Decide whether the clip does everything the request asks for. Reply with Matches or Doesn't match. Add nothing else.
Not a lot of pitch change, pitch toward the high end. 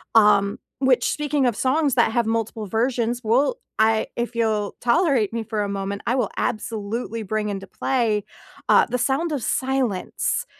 Doesn't match